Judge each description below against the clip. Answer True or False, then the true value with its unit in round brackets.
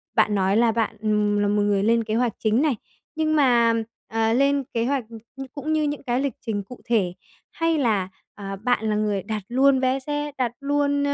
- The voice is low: False (235 Hz)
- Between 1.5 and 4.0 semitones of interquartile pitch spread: False (4.7 semitones)